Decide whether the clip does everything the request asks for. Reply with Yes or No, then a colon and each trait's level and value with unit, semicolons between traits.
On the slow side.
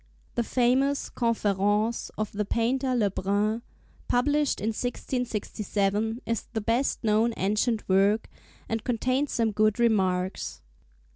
Yes: slow, 120 wpm